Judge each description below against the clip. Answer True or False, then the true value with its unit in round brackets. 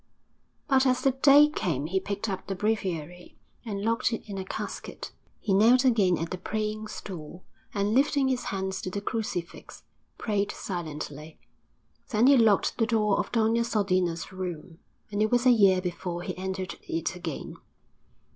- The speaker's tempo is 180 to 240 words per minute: False (165 wpm)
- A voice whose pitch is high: True (200 Hz)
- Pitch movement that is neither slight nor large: True (4.0 semitones)